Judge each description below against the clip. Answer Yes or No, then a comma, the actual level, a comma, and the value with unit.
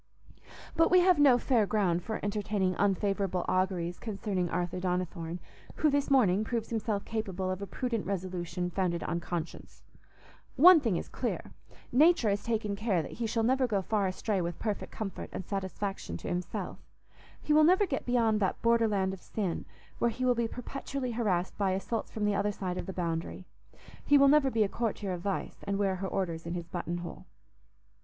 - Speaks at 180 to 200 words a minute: Yes, average, 190 wpm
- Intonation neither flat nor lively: Yes, average, 4.1 semitones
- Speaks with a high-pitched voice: Yes, high, 200 Hz